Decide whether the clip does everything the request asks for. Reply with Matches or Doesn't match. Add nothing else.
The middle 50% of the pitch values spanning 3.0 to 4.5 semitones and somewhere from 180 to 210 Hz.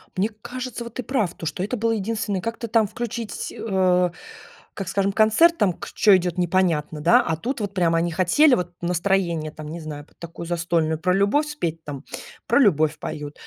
Doesn't match